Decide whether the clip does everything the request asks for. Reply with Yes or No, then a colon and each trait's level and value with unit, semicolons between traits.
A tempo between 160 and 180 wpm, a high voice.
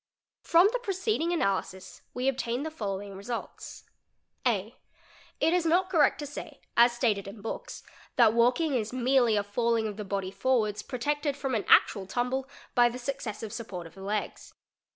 Yes: average, 170 wpm; high, 240 Hz